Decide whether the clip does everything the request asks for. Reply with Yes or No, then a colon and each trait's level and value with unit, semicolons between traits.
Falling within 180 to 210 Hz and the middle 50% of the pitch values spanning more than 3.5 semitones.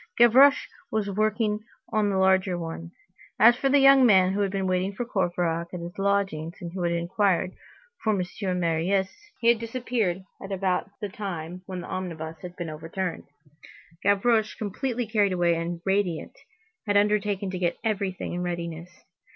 No: high, 190 Hz; average, 3.2 semitones